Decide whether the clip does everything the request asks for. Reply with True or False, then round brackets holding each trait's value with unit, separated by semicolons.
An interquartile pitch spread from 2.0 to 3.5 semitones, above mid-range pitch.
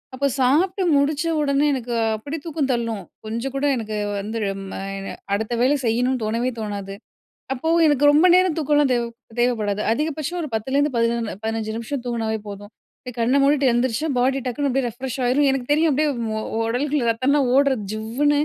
False (4.1 semitones; 255 Hz)